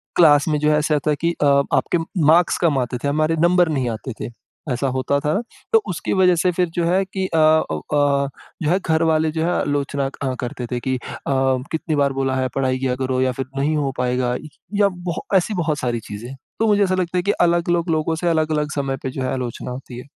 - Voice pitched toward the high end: No, medium, 150 Hz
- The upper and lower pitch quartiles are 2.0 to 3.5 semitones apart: No, average, 4.3 semitones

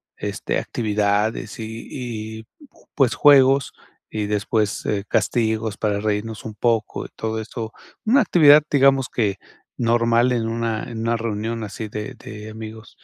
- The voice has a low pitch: Yes, low, 110 Hz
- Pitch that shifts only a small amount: Yes, narrow, 1.7 semitones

